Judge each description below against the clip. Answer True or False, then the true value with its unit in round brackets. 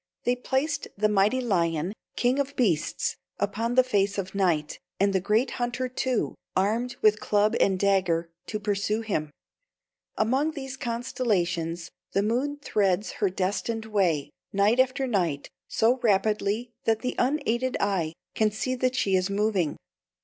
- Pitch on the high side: True (215 Hz)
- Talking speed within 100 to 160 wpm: True (150 wpm)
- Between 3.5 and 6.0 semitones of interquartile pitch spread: True (4.3 semitones)